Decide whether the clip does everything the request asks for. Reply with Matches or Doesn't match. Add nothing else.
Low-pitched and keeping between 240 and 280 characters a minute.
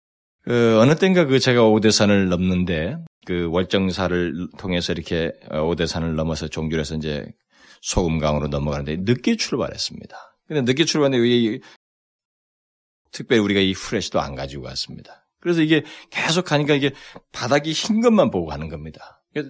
Doesn't match